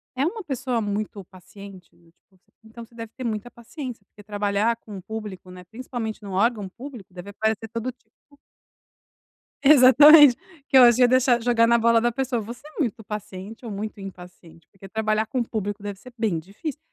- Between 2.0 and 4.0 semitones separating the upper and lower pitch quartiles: Yes, average, 3.4 semitones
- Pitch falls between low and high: No, high, 220 Hz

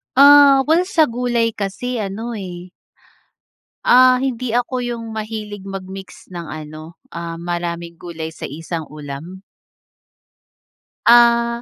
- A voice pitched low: No, high, 205 Hz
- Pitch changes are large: Yes, wide, 6.1 semitones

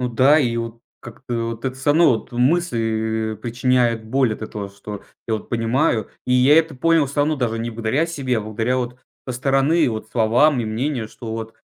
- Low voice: Yes, low, 120 Hz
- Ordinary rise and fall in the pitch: Yes, average, 3.4 semitones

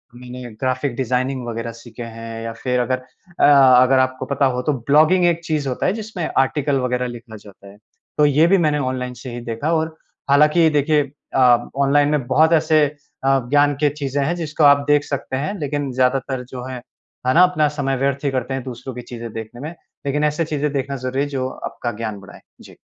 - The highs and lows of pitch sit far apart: No, average, 3.0 semitones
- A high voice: No, low, 135 Hz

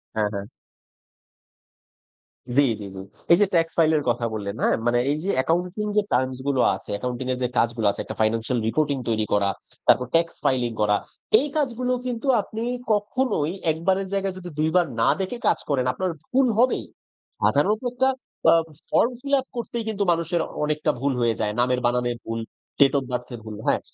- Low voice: No, medium, 150 Hz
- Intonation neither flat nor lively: No, wide, 8.7 semitones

